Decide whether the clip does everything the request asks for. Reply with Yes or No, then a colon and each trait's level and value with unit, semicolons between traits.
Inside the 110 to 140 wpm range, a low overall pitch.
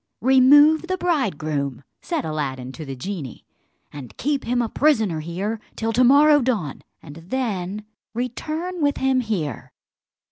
No: slow, 135 wpm; high, 225 Hz